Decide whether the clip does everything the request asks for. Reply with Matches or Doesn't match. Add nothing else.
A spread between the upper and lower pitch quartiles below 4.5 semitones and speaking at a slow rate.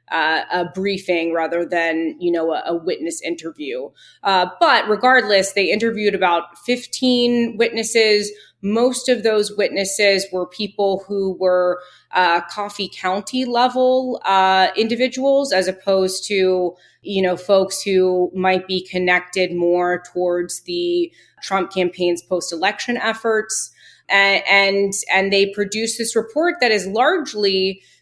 Matches